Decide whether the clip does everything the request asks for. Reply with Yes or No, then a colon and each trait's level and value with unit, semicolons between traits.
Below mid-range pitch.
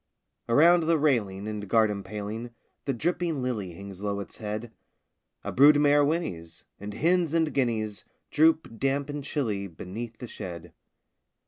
Yes: low, 115 Hz